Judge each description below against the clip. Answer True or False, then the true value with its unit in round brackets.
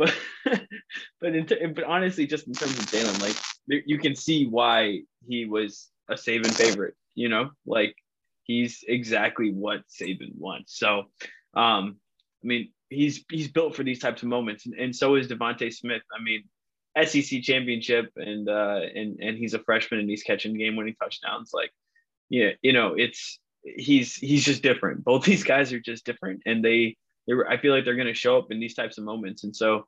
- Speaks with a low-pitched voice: True (120 Hz)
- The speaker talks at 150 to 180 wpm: False (195 wpm)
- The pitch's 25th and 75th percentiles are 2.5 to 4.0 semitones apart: False (4.7 semitones)